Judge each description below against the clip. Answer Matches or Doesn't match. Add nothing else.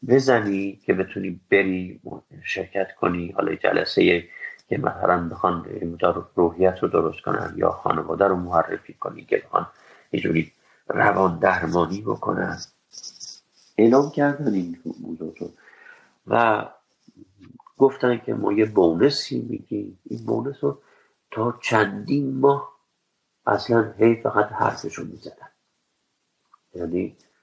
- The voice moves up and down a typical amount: Doesn't match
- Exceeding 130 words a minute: Doesn't match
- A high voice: Doesn't match